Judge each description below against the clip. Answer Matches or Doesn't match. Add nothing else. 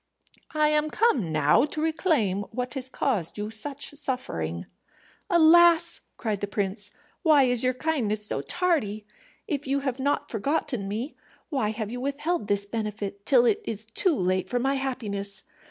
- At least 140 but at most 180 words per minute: Matches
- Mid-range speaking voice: Doesn't match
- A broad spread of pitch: Matches